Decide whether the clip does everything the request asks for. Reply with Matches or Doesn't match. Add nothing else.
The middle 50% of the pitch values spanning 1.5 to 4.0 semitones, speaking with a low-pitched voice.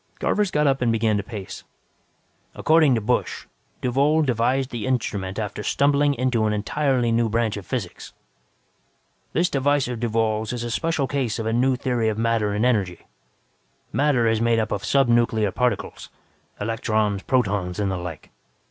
Matches